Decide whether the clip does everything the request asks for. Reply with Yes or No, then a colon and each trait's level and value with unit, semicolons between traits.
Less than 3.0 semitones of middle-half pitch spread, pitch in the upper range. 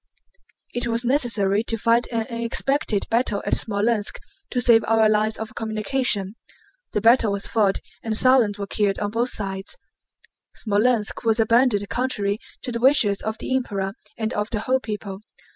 Yes: narrow, 2.6 semitones; high, 220 Hz